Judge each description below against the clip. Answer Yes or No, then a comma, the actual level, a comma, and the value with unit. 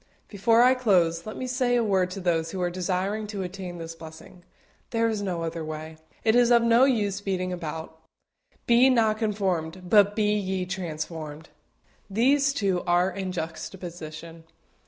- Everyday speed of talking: Yes, average, 170 wpm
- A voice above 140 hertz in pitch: Yes, high, 190 Hz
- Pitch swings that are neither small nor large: Yes, average, 4.5 semitones